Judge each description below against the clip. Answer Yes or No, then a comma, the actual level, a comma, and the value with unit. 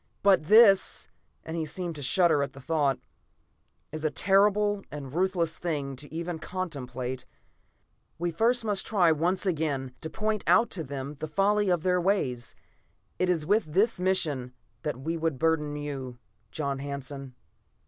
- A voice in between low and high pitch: Yes, medium, 160 Hz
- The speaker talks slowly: No, average, 160 wpm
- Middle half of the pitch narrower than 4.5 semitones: No, average, 5.0 semitones